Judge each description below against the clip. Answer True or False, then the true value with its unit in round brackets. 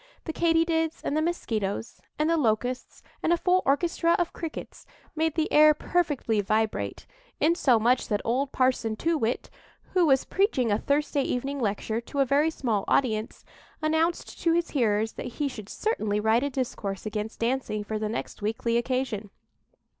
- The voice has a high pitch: True (260 Hz)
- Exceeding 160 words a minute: True (170 wpm)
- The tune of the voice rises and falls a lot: True (6.4 semitones)